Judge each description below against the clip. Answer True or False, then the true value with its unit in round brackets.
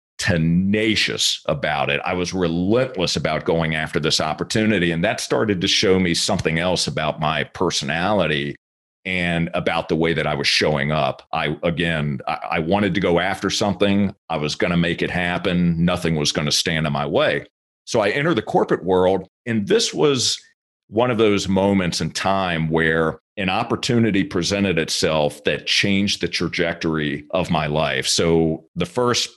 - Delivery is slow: False (170 wpm)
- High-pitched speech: False (90 Hz)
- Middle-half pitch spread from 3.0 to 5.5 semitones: True (3.3 semitones)